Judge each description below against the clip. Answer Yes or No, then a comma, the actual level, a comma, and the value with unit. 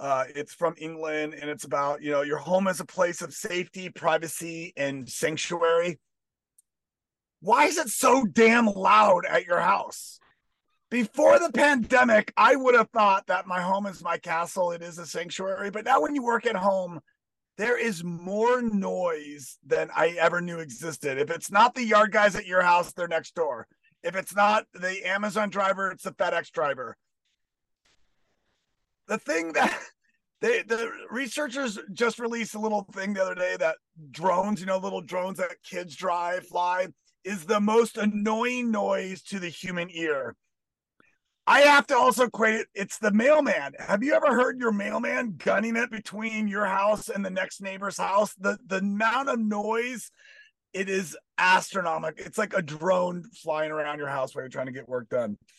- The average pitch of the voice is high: Yes, high, 195 Hz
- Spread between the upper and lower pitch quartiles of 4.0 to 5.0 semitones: Yes, average, 4.6 semitones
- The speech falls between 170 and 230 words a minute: Yes, average, 175 wpm